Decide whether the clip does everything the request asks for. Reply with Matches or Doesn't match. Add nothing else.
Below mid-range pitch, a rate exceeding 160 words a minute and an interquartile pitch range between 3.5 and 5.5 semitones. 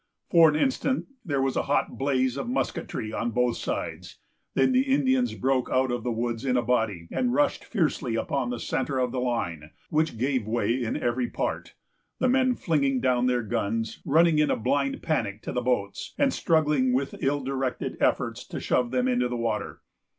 Matches